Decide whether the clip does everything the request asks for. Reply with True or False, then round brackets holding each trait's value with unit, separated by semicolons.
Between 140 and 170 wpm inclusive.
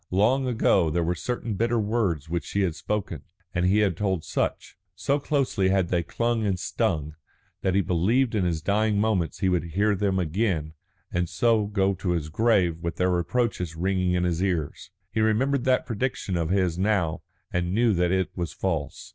False (190 wpm)